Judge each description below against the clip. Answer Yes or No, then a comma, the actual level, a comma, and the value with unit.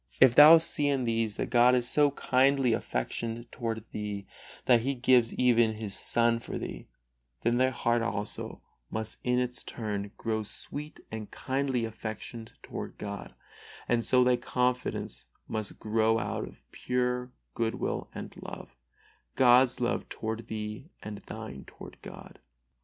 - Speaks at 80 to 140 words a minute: No, average, 150 wpm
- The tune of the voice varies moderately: No, narrow, 2.3 semitones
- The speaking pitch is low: Yes, low, 120 Hz